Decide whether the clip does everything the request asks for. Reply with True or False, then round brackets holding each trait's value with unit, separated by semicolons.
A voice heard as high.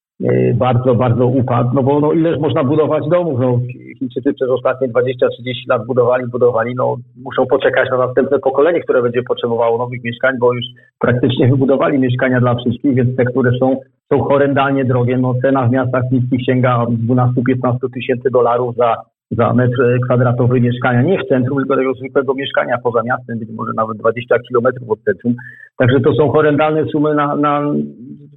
False (125 Hz)